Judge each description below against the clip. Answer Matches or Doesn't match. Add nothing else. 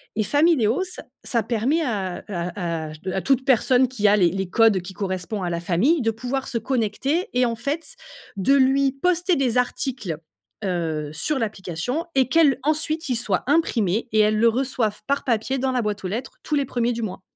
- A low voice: Doesn't match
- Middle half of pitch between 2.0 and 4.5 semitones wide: Doesn't match